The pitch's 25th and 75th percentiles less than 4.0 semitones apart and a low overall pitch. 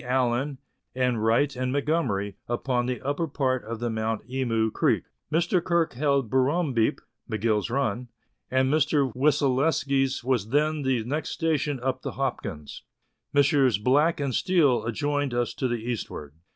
Yes: average, 3.4 semitones; low, 130 Hz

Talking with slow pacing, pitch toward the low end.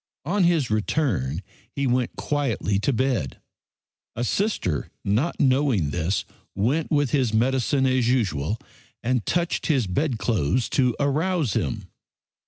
Yes: slow, 125 wpm; low, 125 Hz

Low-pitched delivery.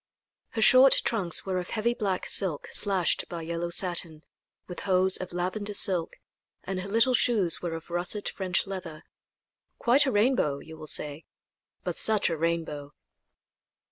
No: medium, 185 Hz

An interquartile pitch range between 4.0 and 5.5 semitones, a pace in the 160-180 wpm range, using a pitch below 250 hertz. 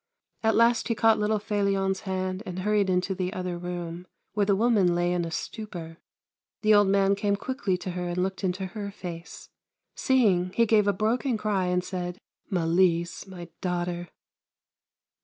No: average, 2.8 semitones; average, 175 wpm; high, 190 Hz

